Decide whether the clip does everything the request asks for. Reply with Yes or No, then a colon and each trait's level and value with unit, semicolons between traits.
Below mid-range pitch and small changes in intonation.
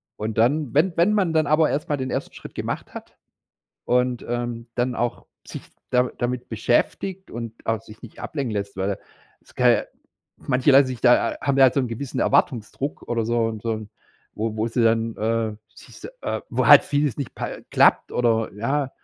No: low, 120 Hz; average, 3.7 semitones